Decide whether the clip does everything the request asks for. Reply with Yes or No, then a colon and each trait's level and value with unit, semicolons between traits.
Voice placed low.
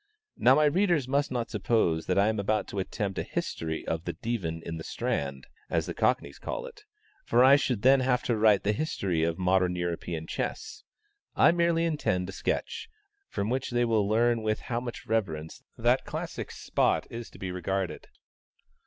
Yes: low, 110 Hz